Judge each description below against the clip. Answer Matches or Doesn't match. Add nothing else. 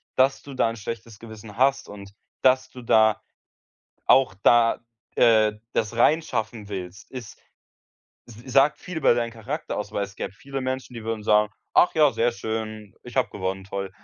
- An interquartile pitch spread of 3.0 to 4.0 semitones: Matches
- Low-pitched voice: Matches